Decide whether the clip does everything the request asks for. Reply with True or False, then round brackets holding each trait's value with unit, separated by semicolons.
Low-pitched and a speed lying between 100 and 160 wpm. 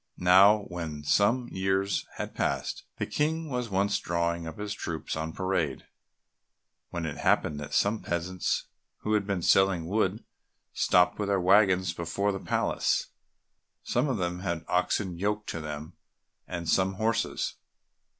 True (95 Hz; 150 wpm)